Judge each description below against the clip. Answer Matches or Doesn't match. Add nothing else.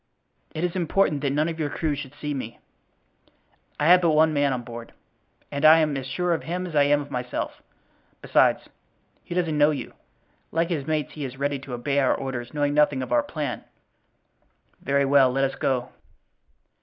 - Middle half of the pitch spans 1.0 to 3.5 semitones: Matches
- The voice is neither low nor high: Matches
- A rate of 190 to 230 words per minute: Matches